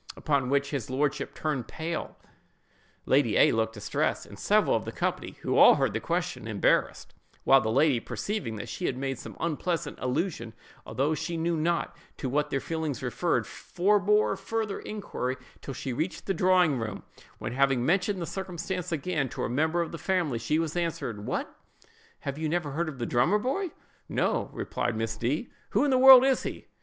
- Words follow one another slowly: No, average, 185 wpm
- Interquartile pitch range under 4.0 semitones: No, wide, 5.6 semitones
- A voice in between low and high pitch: Yes, medium, 155 Hz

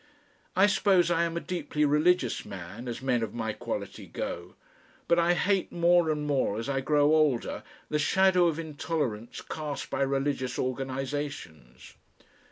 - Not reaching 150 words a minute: No, average, 155 wpm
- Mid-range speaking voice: Yes, medium, 145 Hz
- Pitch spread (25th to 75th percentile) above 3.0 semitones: Yes, average, 4.9 semitones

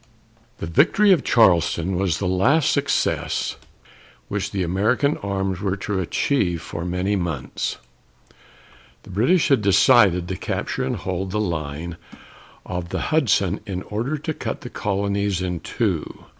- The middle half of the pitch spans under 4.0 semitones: Yes, average, 3.2 semitones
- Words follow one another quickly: No, average, 140 wpm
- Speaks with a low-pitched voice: Yes, very low, 95 Hz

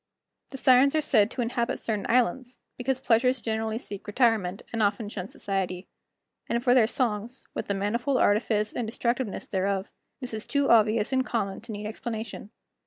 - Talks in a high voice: Yes, high, 225 Hz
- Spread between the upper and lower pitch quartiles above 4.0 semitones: No, average, 3.3 semitones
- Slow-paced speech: No, average, 175 wpm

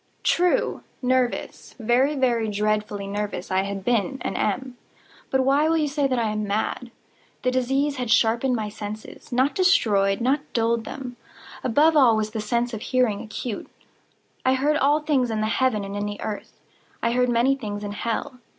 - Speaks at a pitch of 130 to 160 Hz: No, high, 240 Hz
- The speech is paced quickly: No, average, 170 wpm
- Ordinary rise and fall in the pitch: Yes, average, 3.8 semitones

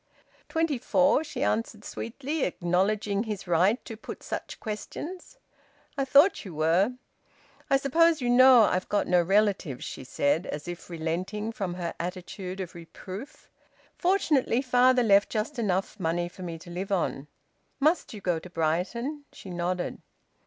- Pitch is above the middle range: Yes, high, 205 Hz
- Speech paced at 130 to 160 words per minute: Yes, average, 150 wpm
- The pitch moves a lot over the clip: Yes, wide, 6.4 semitones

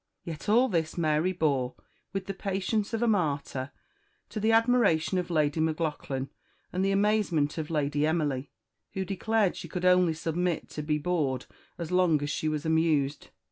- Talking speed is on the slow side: No, average, 170 wpm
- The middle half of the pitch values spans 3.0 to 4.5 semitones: Yes, average, 4.2 semitones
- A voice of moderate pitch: Yes, medium, 165 Hz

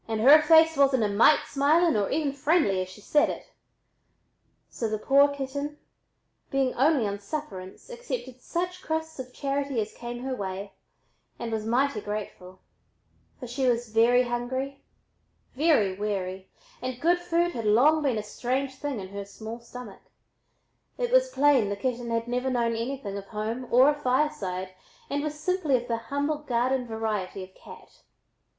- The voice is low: No, very high, 250 Hz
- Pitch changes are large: No, average, 5.0 semitones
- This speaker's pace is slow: No, average, 170 wpm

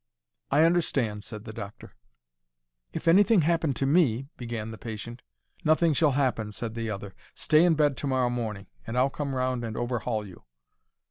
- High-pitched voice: No, low, 125 Hz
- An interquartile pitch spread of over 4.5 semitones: Yes, average, 5.2 semitones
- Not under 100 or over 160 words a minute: No, average, 175 wpm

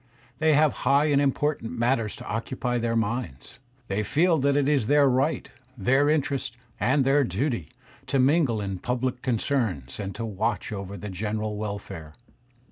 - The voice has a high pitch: No, low, 120 Hz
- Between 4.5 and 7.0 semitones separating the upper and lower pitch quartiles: Yes, average, 5.1 semitones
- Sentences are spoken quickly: No, average, 160 wpm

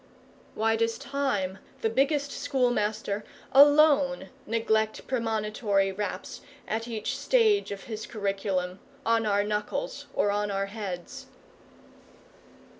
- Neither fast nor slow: No, slow, 105 wpm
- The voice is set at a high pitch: Yes, high, 220 Hz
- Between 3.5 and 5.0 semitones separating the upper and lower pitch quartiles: Yes, average, 4.2 semitones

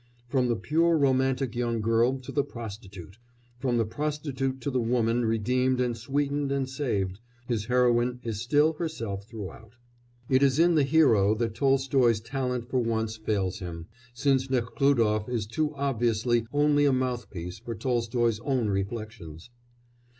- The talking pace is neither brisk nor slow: Yes, average, 150 wpm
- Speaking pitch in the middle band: No, low, 120 Hz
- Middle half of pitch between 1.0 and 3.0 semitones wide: No, average, 3.4 semitones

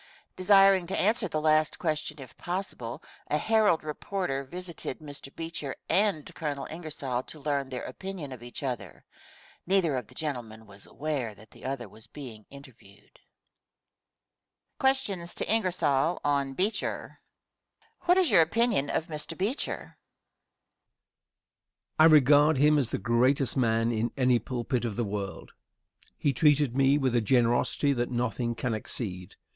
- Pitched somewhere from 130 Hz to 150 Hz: Yes, medium, 140 Hz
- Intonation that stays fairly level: No, average, 5.3 semitones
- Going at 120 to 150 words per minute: Yes, average, 140 wpm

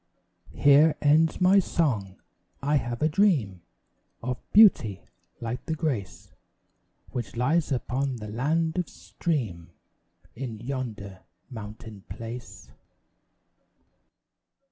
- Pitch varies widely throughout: Yes, wide, 6.0 semitones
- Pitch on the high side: No, low, 125 Hz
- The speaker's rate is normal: No, slow, 100 wpm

